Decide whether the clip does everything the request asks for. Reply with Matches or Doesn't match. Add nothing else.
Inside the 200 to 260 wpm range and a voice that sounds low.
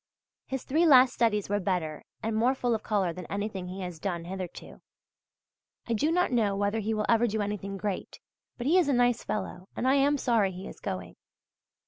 Doesn't match